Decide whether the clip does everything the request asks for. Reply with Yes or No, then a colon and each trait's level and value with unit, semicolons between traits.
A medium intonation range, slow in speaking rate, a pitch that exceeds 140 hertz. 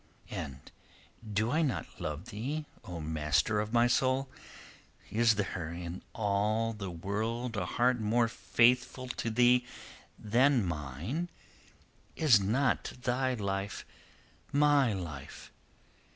No: average, 4.3 semitones; slow, 115 wpm; low, 110 Hz